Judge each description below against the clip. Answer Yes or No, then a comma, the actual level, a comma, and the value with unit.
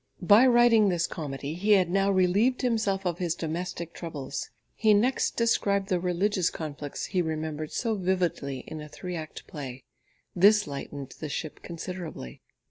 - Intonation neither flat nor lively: Yes, average, 4.4 semitones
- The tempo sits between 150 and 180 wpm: Yes, average, 155 wpm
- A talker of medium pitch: Yes, medium, 180 Hz